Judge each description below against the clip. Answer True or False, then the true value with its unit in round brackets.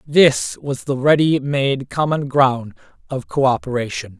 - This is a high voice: False (135 Hz)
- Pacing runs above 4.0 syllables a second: False (3.8 syllables/s)